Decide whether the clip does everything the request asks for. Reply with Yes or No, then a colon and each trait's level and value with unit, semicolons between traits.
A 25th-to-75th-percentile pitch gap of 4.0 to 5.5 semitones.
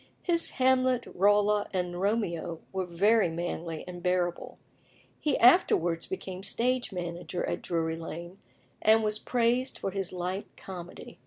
Yes: average, 4.4 semitones